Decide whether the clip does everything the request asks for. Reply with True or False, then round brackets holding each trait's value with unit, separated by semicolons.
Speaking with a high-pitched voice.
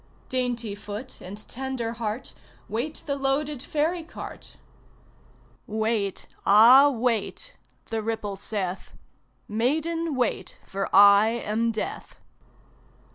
True (230 Hz)